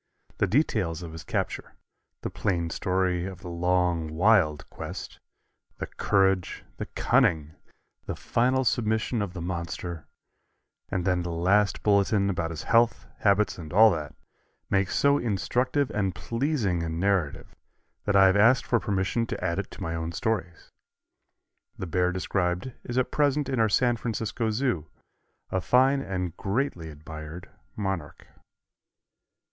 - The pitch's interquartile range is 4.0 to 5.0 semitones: Yes, average, 4.7 semitones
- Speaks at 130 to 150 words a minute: Yes, average, 145 wpm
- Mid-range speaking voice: No, very low, 95 Hz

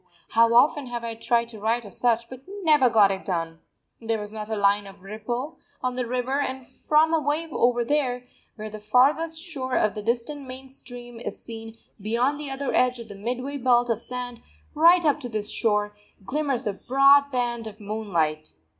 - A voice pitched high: Yes, high, 240 Hz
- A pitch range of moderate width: Yes, average, 3.8 semitones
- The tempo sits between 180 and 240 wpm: Yes, average, 195 wpm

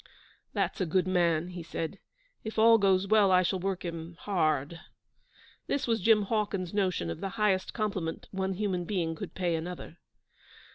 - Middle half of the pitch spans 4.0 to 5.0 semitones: No, average, 3.1 semitones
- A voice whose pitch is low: No, medium, 185 Hz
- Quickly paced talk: No, average, 165 wpm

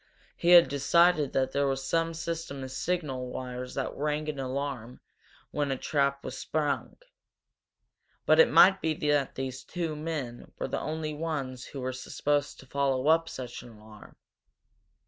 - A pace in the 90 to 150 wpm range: No, average, 165 wpm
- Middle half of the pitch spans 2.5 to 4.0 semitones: Yes, average, 3.3 semitones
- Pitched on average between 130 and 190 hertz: Yes, medium, 140 Hz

